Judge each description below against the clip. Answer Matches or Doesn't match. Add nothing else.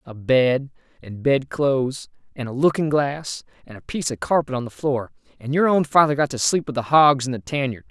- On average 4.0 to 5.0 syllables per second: Doesn't match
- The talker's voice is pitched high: Doesn't match